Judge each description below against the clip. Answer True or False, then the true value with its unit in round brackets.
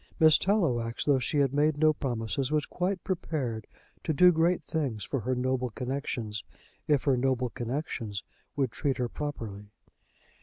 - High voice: False (135 Hz)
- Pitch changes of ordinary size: True (4.2 semitones)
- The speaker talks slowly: False (155 wpm)